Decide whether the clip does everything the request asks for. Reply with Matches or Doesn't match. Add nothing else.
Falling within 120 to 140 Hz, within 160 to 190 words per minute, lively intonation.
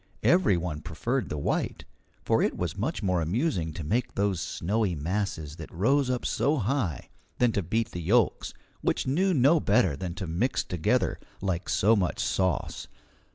Doesn't match